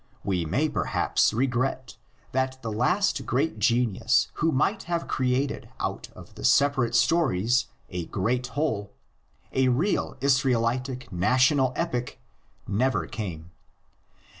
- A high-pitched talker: No, low, 125 Hz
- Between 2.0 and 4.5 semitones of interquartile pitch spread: Yes, average, 3.3 semitones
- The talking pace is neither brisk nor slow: No, slow, 115 wpm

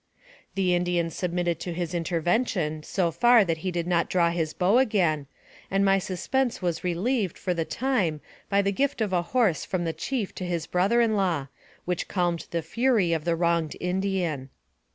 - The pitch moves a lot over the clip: No, average, 2.8 semitones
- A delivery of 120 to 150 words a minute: No, average, 185 wpm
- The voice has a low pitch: No, medium, 180 Hz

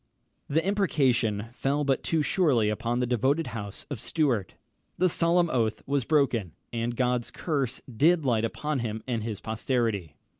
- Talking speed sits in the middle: Yes, average, 160 wpm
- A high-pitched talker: No, low, 125 Hz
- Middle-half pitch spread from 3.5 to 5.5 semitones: Yes, average, 4.6 semitones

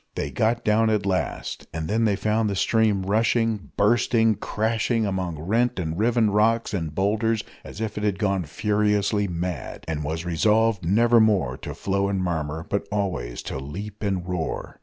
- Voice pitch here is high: No, low, 100 Hz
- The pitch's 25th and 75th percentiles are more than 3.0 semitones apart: Yes, average, 3.6 semitones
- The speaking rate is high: No, average, 175 wpm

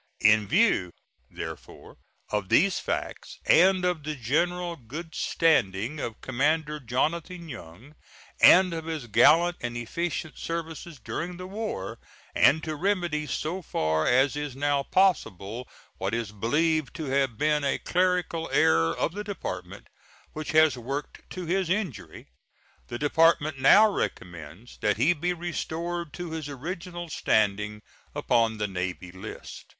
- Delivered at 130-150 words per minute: Yes, average, 140 wpm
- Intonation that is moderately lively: No, wide, 6.8 semitones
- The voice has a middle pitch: Yes, medium, 150 Hz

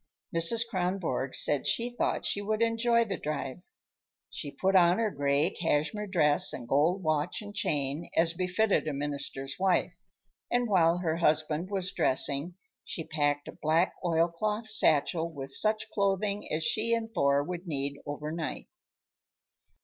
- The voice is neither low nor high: Yes, medium, 170 Hz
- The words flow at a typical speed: Yes, average, 150 wpm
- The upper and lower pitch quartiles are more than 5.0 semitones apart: Yes, wide, 5.4 semitones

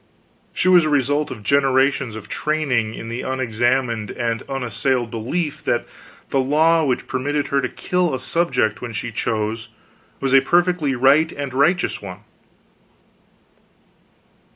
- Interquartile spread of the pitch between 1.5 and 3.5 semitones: No, average, 4.1 semitones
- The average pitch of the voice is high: No, low, 135 Hz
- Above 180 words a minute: No, average, 140 wpm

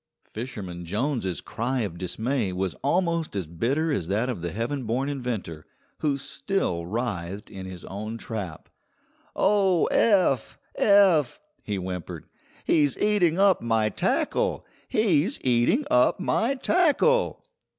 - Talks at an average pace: No, slow, 130 wpm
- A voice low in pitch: Yes, low, 125 Hz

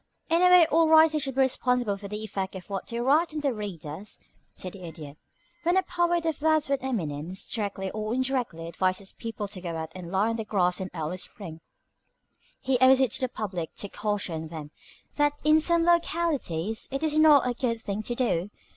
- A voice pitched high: Yes, high, 220 Hz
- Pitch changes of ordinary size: No, wide, 7.8 semitones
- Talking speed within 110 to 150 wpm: No, fast, 205 wpm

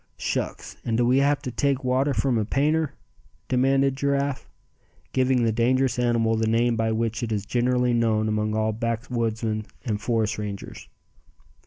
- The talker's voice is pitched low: Yes, low, 120 Hz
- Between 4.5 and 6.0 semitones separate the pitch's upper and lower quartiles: No, average, 2.8 semitones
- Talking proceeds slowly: No, average, 160 wpm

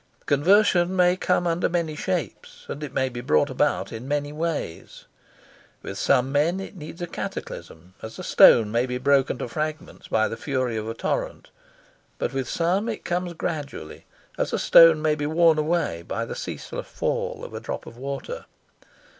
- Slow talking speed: No, average, 180 wpm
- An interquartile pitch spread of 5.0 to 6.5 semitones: Yes, wide, 5.6 semitones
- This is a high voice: No, medium, 150 Hz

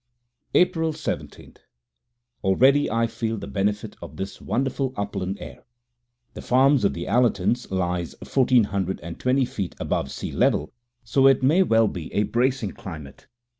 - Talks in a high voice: No, low, 115 Hz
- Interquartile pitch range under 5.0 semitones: No, wide, 5.4 semitones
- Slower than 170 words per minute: Yes, average, 150 wpm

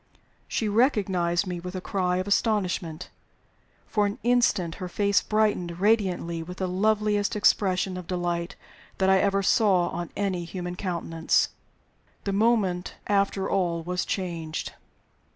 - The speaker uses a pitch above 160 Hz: Yes, medium, 185 Hz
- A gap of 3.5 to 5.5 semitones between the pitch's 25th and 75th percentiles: No, narrow, 2.6 semitones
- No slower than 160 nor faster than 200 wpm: No, slow, 135 wpm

